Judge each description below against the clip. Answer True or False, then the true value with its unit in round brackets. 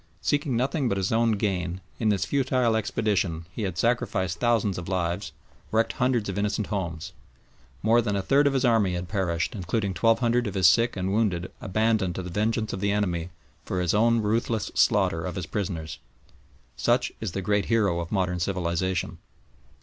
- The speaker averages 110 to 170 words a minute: False (185 wpm)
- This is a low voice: True (100 Hz)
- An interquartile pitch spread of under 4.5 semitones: True (4.1 semitones)